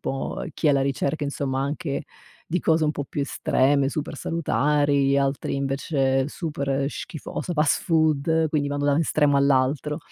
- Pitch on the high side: No, medium, 145 Hz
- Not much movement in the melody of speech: Yes, narrow, 1.8 semitones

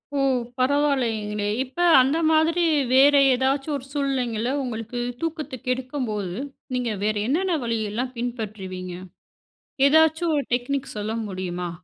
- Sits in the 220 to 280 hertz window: Yes, very high, 255 Hz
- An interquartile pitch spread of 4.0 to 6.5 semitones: Yes, average, 4.9 semitones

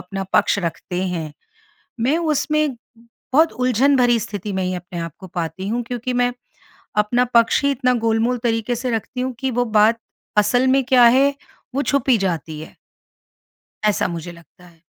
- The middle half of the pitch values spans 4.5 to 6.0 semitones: Yes, average, 5.2 semitones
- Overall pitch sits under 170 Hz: No, high, 230 Hz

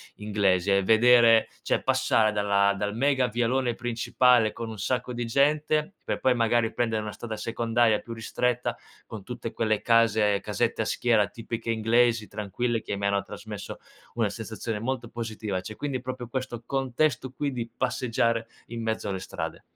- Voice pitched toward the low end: Yes, low, 115 Hz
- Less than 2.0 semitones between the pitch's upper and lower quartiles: No, narrow, 2.4 semitones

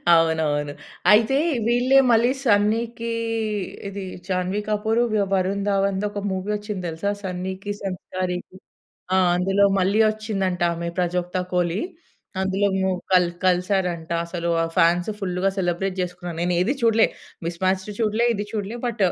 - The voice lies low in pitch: No, high, 190 Hz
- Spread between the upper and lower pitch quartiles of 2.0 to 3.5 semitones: Yes, average, 2.7 semitones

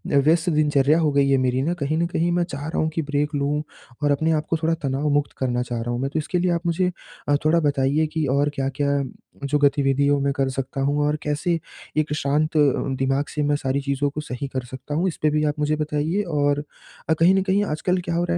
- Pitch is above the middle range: No, medium, 145 Hz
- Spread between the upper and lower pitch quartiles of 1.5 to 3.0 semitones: Yes, narrow, 2.4 semitones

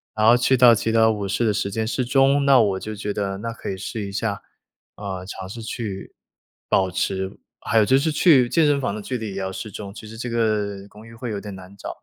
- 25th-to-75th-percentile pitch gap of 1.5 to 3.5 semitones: Yes, average, 3.2 semitones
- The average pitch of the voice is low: Yes, low, 110 Hz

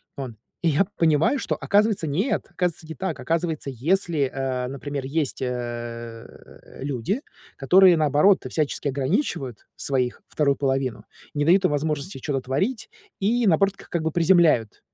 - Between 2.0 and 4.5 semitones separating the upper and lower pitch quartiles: No, average, 5.1 semitones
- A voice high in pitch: No, medium, 150 Hz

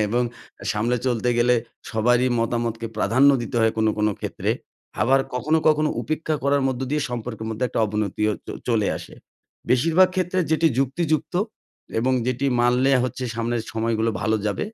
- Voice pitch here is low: Yes, low, 120 Hz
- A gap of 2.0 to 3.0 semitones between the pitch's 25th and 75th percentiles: No, average, 3.6 semitones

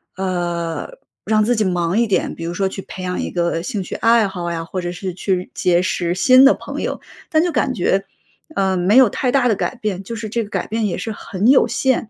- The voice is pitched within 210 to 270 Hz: No, high, 195 Hz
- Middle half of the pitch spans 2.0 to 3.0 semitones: No, average, 4.4 semitones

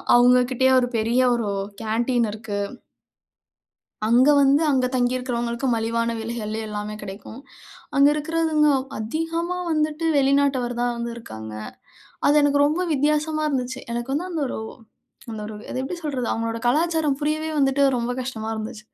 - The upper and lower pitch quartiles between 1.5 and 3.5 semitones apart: No, average, 4.3 semitones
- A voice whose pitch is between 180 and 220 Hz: No, very high, 255 Hz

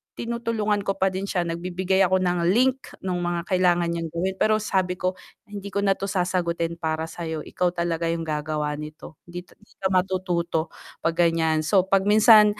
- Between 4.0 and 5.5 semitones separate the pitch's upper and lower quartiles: No, narrow, 2.4 semitones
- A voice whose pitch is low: No, medium, 180 Hz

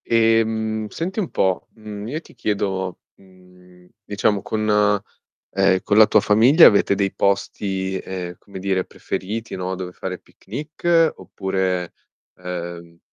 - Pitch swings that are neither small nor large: Yes, average, 3.0 semitones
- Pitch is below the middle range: Yes, low, 100 Hz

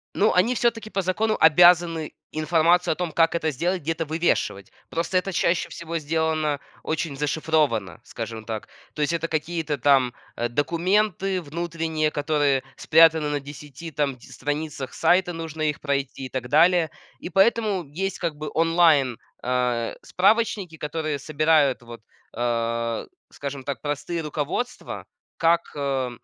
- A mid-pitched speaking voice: Yes, medium, 155 Hz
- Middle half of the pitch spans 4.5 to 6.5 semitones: No, average, 3.4 semitones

